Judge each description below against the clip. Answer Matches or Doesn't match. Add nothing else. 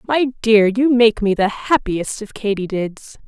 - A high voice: Matches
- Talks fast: Doesn't match